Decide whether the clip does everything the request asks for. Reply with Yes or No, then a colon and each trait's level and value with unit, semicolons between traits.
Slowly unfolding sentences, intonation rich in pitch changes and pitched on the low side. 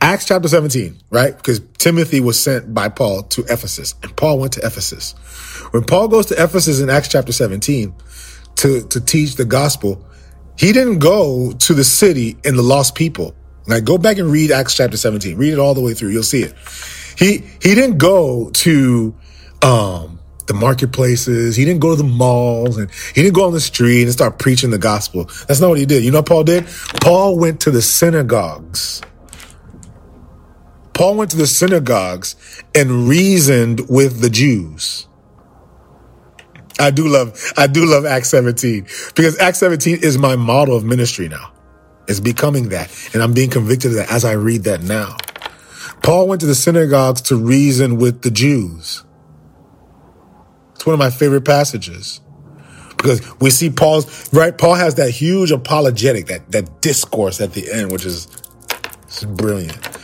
No: average, 175 wpm; wide, 6.5 semitones; low, 125 Hz